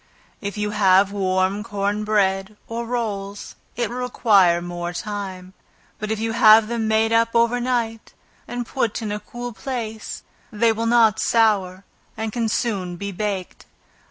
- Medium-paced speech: Yes, average, 155 wpm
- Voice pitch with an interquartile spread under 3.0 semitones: Yes, narrow, 2.6 semitones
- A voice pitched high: Yes, high, 215 Hz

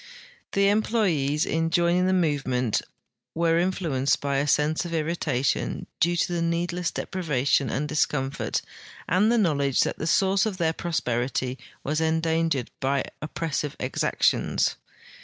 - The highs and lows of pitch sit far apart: No, average, 3.7 semitones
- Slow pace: Yes, slow, 130 wpm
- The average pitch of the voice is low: No, medium, 160 Hz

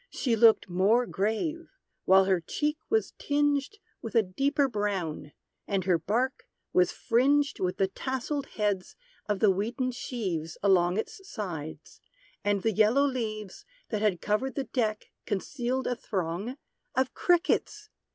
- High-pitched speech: Yes, high, 220 Hz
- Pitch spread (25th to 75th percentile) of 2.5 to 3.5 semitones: No, wide, 5.5 semitones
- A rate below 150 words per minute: Yes, average, 140 wpm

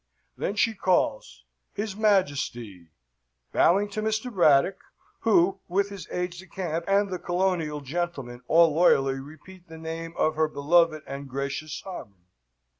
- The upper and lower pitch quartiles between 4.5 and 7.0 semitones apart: Yes, average, 5.1 semitones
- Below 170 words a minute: Yes, average, 140 wpm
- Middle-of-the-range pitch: Yes, medium, 170 Hz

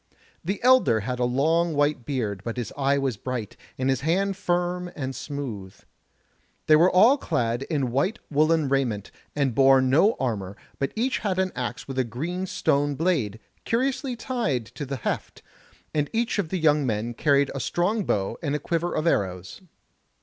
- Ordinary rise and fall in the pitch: No, wide, 6.0 semitones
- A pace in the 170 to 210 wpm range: Yes, average, 180 wpm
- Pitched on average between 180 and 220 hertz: No, medium, 140 Hz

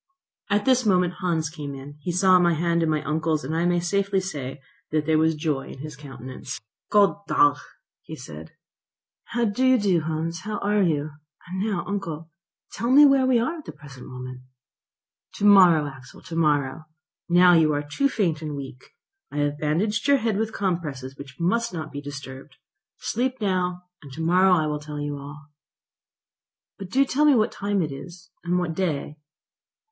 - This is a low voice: No, medium, 170 Hz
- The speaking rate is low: No, average, 185 wpm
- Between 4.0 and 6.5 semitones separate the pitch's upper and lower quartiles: Yes, average, 5.2 semitones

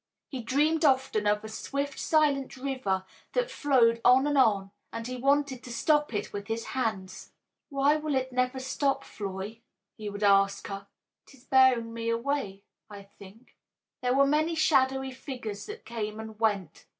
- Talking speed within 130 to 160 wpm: No, average, 170 wpm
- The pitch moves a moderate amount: Yes, average, 4.6 semitones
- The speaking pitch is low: No, very high, 250 Hz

